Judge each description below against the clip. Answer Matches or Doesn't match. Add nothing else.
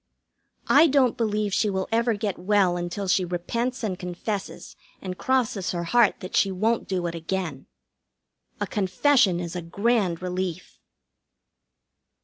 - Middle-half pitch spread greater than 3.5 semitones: Matches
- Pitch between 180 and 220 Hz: Matches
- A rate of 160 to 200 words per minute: Doesn't match